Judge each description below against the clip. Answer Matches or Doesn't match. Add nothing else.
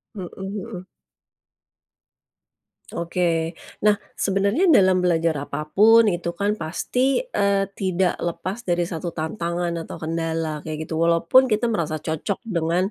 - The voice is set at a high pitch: Doesn't match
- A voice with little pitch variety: Doesn't match